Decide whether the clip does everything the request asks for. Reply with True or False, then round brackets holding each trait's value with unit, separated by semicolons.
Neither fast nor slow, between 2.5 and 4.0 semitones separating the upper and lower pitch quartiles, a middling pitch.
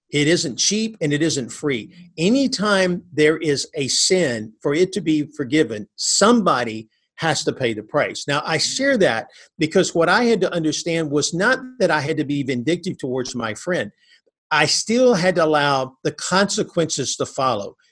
False (175 wpm; 4.5 semitones; 160 Hz)